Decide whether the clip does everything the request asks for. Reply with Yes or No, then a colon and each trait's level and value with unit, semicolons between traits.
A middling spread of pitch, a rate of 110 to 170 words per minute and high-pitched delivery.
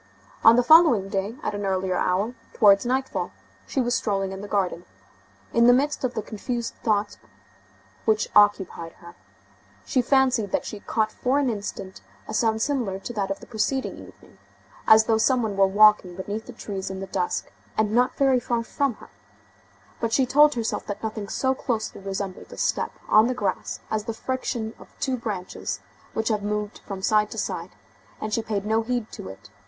No: average, 3.6 semitones; average, 190 wpm; high, 220 Hz